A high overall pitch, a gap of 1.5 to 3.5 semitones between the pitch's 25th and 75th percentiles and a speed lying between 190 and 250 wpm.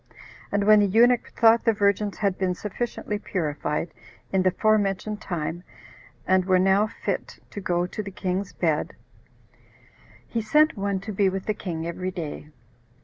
No: high, 195 Hz; average, 2.7 semitones; average, 165 wpm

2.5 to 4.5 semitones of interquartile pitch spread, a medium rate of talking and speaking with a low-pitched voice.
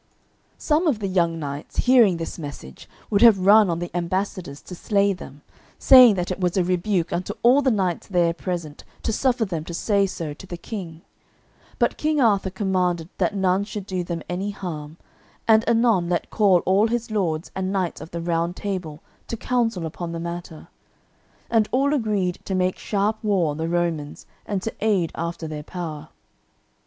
No: average, 3.7 semitones; average, 185 wpm; medium, 185 Hz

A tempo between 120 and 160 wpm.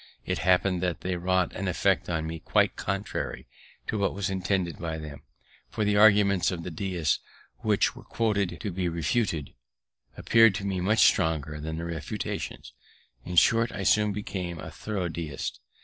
No: average, 170 wpm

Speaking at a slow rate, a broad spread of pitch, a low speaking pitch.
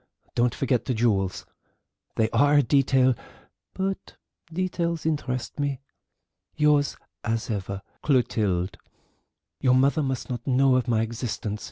No: slow, 125 wpm; average, 4.1 semitones; low, 130 Hz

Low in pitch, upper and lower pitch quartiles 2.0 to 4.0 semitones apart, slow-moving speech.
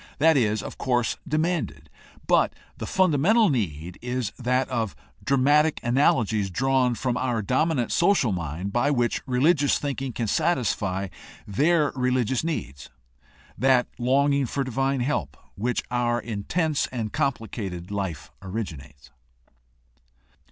No: low, 125 Hz; average, 4.9 semitones; slow, 125 wpm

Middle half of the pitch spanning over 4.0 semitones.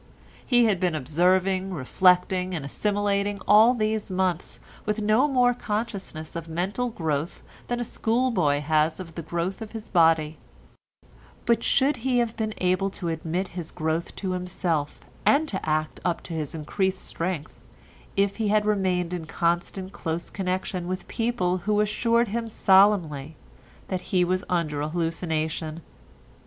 Yes: average, 4.4 semitones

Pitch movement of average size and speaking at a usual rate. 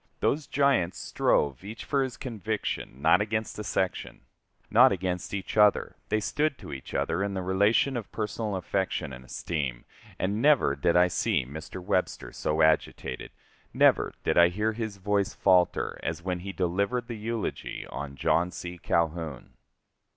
Yes: average, 4.1 semitones; average, 160 wpm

